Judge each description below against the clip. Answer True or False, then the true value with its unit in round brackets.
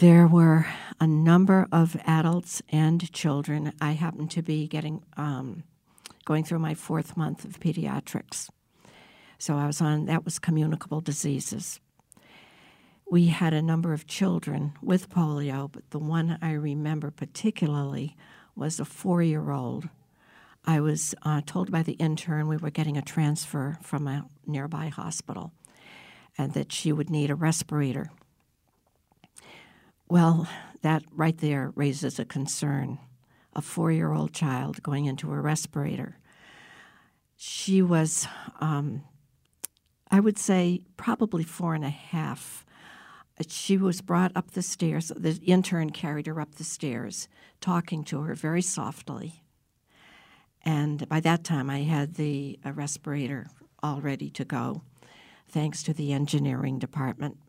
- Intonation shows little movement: True (2.3 semitones)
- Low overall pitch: False (155 Hz)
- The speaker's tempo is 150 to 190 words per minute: False (140 wpm)